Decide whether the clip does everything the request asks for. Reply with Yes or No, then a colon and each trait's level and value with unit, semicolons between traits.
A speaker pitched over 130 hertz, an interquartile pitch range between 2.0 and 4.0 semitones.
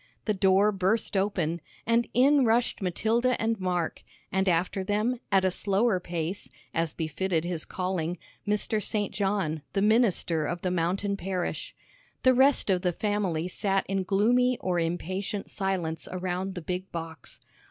Yes: high, 190 Hz; average, 3.0 semitones